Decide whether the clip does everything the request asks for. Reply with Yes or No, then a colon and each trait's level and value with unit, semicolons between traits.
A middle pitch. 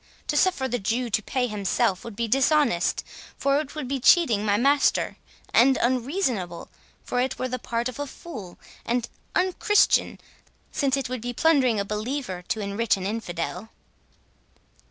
No: high, 245 Hz